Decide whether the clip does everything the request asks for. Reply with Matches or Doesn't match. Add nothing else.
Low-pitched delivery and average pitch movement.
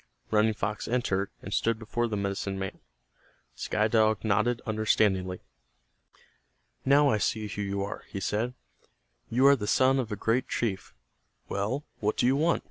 Matches